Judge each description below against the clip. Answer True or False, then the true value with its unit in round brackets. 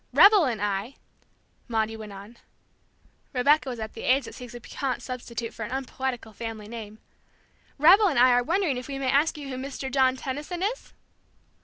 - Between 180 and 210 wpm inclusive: True (185 wpm)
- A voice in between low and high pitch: False (255 Hz)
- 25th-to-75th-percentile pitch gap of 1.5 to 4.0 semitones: True (3.5 semitones)